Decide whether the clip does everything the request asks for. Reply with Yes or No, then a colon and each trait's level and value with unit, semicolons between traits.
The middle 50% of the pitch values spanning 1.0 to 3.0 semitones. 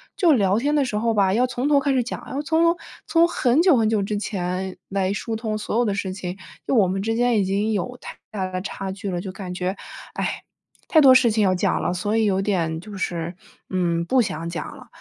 No: average, 4.7 semitones